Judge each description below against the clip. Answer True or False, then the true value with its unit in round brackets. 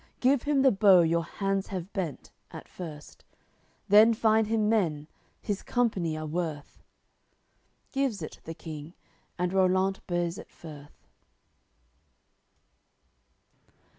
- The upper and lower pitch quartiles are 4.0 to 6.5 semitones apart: True (4.7 semitones)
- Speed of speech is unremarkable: False (115 wpm)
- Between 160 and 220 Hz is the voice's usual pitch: True (185 Hz)